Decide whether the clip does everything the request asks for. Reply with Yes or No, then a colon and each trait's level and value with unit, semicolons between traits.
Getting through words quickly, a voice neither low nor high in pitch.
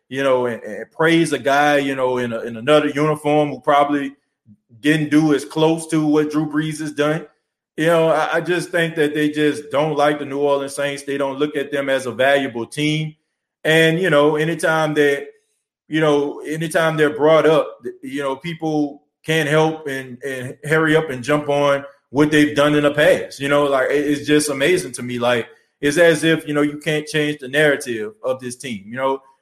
Yes: fast, 210 wpm; medium, 150 Hz